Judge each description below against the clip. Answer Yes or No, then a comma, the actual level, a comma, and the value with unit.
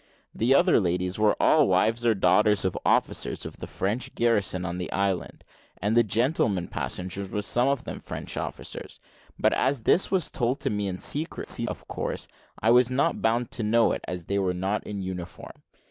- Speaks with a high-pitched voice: No, low, 105 Hz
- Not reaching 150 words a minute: No, average, 190 wpm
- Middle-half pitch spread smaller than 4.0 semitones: No, average, 4.4 semitones